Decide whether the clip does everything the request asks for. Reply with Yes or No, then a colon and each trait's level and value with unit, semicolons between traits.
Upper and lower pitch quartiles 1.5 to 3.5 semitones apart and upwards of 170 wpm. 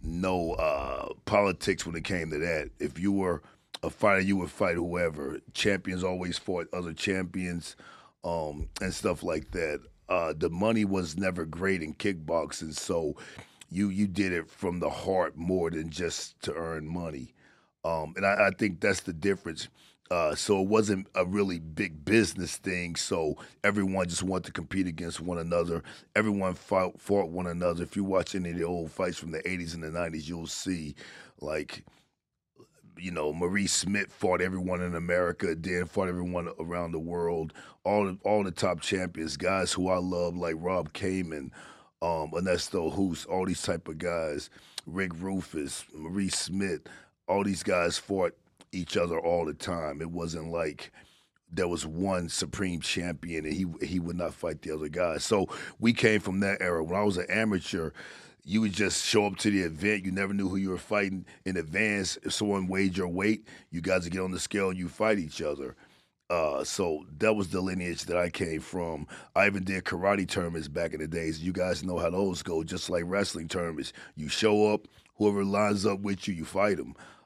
Yes: narrow, 2.6 semitones; average, 190 wpm